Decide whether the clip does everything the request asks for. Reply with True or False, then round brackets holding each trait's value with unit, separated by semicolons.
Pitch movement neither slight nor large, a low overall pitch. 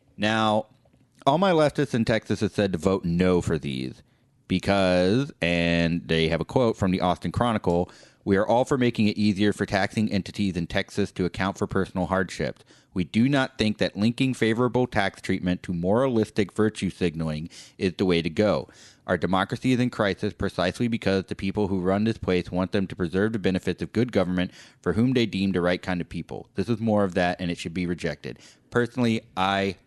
True (3.6 semitones; 95 Hz)